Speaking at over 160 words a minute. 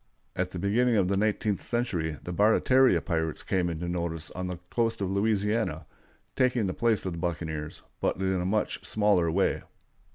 Yes: average, 175 wpm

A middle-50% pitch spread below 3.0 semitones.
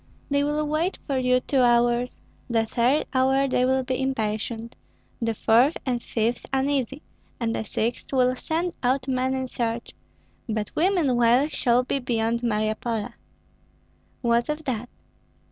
Yes: narrow, 2.5 semitones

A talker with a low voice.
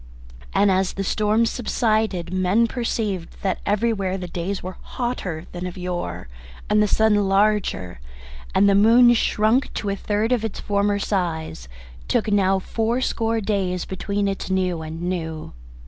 No: high, 200 Hz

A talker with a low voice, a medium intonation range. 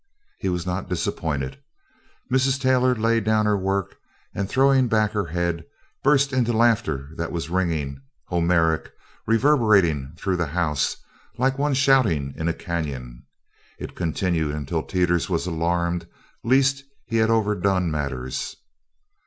No: very low, 90 Hz; wide, 5.9 semitones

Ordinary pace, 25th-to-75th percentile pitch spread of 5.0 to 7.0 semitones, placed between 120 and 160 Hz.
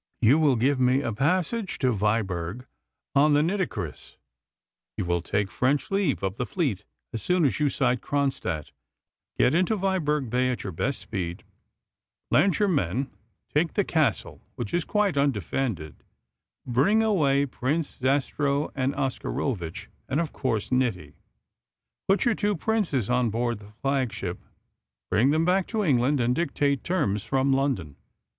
Yes: average, 150 wpm; average, 5.3 semitones; low, 135 Hz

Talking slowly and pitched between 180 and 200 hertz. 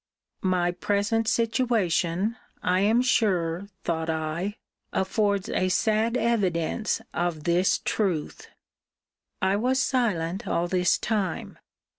Yes: slow, 105 wpm; high, 190 Hz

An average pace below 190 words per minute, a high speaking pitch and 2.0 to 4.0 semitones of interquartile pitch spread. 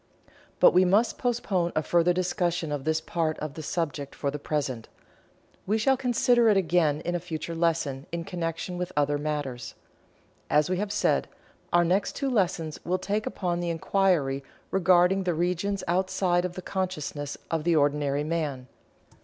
No: average, 170 wpm; medium, 170 Hz; average, 3.6 semitones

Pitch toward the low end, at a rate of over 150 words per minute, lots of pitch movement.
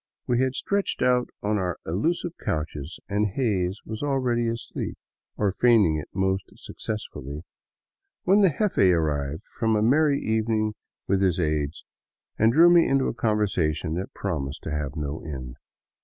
Yes: low, 105 Hz; average, 160 wpm; wide, 7.5 semitones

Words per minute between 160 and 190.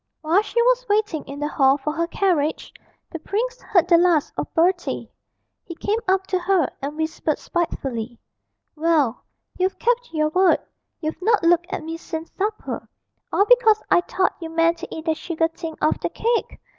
Yes: average, 180 wpm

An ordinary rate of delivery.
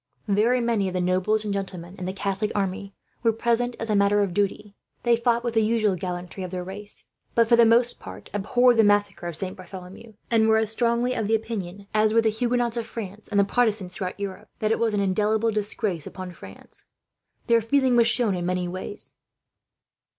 No: fast, 210 wpm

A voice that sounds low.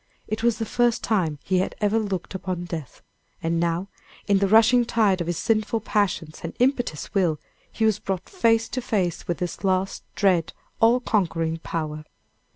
No: high, 195 Hz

